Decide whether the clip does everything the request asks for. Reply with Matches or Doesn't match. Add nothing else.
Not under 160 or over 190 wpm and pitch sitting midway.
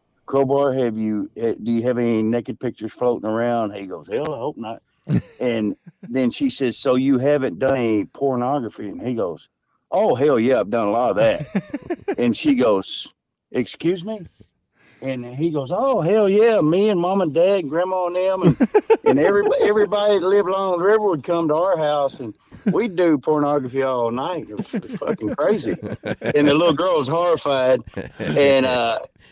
Matches